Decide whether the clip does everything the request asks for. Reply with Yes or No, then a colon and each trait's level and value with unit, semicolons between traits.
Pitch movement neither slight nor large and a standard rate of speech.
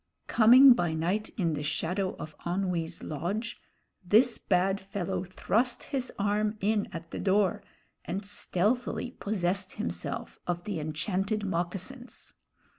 No: average, 3.5 semitones; slow, 125 wpm